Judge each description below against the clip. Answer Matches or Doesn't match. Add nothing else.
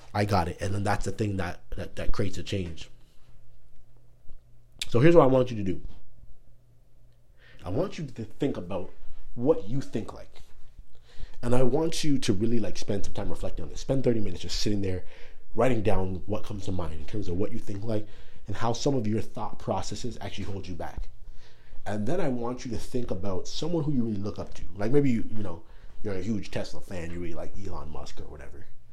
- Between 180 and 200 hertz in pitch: Doesn't match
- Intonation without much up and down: Doesn't match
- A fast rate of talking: Matches